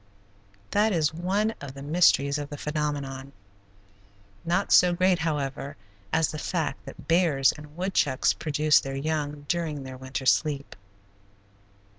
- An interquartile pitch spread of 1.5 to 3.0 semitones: No, average, 3.4 semitones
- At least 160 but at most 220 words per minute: No, slow, 135 wpm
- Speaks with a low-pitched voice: No, medium, 150 Hz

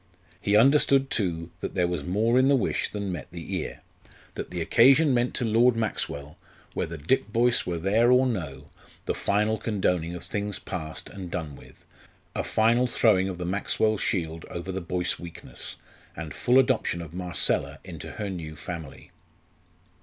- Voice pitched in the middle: No, very low, 95 Hz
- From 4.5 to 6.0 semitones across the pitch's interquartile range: Yes, average, 5.0 semitones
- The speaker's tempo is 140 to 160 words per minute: No, average, 170 wpm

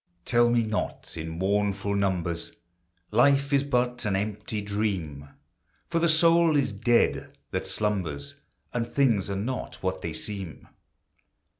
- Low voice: Yes, low, 105 Hz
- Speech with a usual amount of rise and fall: Yes, average, 4.4 semitones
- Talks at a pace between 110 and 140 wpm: Yes, slow, 135 wpm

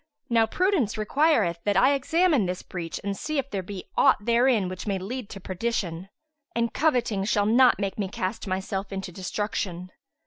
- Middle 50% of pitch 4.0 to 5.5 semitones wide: Yes, average, 4.4 semitones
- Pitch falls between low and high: No, high, 205 Hz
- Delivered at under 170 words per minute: No, average, 175 wpm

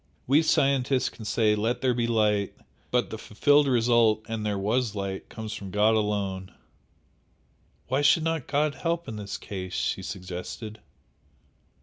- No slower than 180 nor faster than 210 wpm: No, average, 150 wpm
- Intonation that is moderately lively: Yes, average, 4.1 semitones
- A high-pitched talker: No, low, 110 Hz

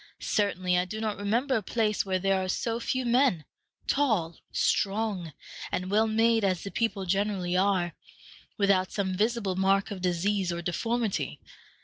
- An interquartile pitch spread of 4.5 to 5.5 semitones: No, average, 3.1 semitones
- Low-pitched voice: No, high, 200 Hz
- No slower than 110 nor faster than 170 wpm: Yes, average, 155 wpm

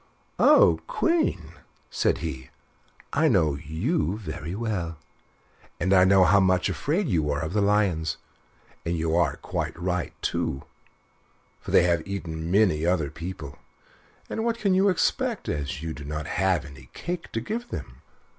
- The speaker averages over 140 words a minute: Yes, average, 155 wpm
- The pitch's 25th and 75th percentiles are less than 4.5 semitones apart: No, average, 5.2 semitones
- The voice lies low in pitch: Yes, very low, 90 Hz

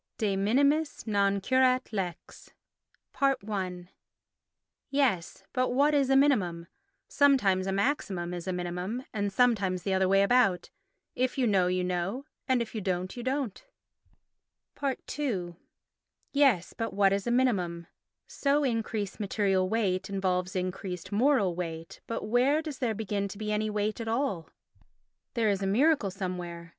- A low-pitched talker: No, high, 205 Hz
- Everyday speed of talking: Yes, average, 150 wpm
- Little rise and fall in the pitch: No, wide, 5.4 semitones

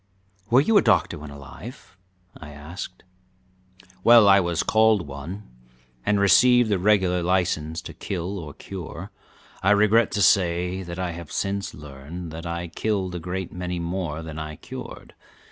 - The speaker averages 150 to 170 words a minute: Yes, average, 160 wpm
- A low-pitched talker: Yes, very low, 90 Hz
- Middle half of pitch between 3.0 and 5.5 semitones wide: Yes, average, 3.4 semitones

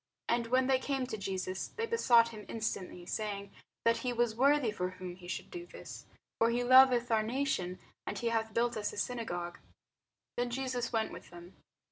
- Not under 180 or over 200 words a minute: Yes, average, 190 wpm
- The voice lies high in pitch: Yes, high, 230 Hz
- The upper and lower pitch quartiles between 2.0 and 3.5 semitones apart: No, average, 4.0 semitones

